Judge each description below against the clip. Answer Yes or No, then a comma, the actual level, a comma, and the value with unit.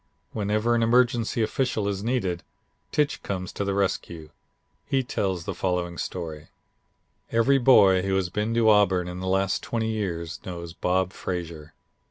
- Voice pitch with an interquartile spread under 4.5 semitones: Yes, average, 4.0 semitones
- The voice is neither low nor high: No, very low, 95 Hz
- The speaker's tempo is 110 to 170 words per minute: Yes, average, 155 wpm